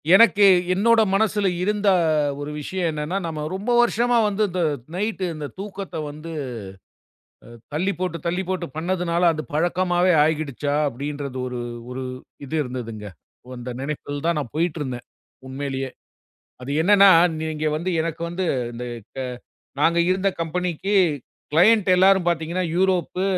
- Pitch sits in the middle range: Yes, medium, 170 Hz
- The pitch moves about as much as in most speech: Yes, average, 4.1 semitones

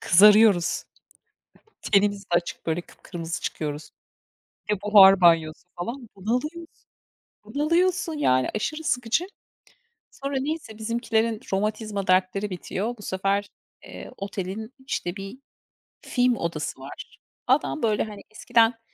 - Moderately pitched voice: No, high, 210 Hz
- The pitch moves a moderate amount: Yes, average, 4.5 semitones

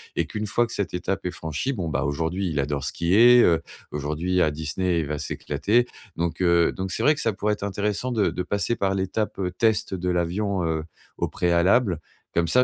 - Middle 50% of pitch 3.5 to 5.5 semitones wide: Yes, average, 3.8 semitones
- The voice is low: Yes, very low, 90 Hz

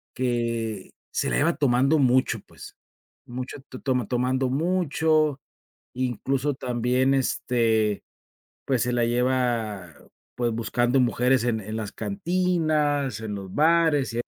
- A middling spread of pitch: Yes, average, 3.4 semitones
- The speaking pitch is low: Yes, low, 125 Hz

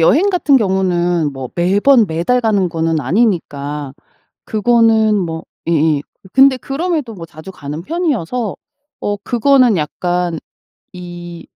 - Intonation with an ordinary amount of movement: No, wide, 6.6 semitones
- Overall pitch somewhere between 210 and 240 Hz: No, medium, 185 Hz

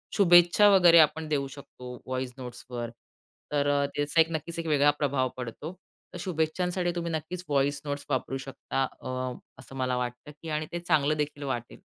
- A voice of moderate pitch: Yes, medium, 145 Hz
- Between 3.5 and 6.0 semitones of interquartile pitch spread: Yes, average, 3.9 semitones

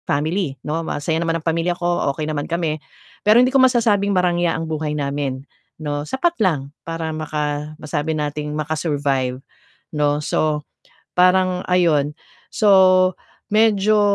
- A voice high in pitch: No, medium, 160 Hz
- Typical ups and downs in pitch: Yes, average, 3.6 semitones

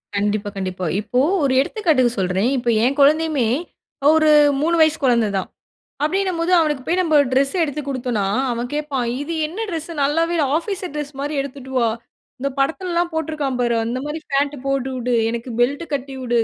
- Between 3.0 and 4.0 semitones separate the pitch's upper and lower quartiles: No, average, 4.5 semitones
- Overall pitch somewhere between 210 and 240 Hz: No, very high, 280 Hz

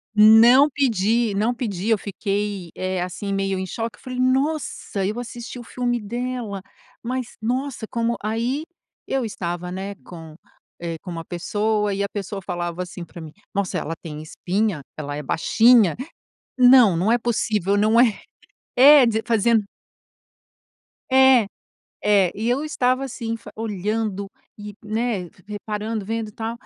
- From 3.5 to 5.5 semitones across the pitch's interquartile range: Yes, average, 3.8 semitones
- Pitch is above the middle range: Yes, high, 215 Hz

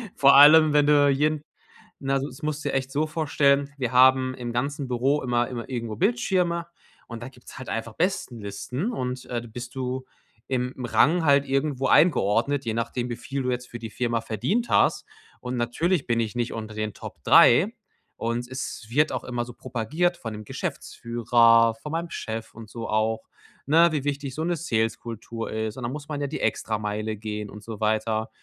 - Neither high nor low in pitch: No, low, 125 Hz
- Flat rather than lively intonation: No, average, 3.9 semitones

